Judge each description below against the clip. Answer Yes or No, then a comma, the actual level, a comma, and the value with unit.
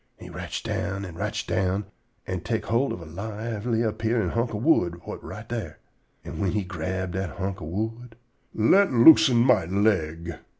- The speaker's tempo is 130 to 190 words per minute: Yes, average, 180 wpm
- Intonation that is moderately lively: Yes, average, 4.0 semitones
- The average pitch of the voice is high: No, low, 105 Hz